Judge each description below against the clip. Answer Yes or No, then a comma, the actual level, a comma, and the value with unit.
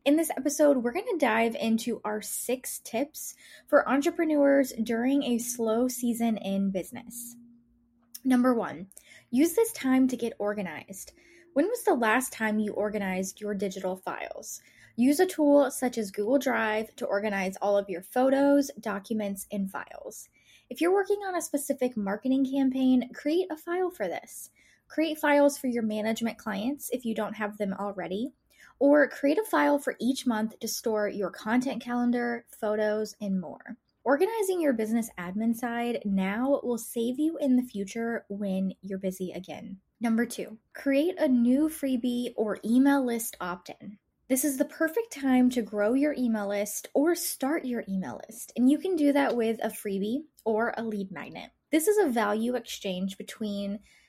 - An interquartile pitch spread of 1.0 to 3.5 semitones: No, average, 4.9 semitones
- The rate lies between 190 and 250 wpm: No, average, 170 wpm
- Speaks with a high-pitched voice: Yes, high, 240 Hz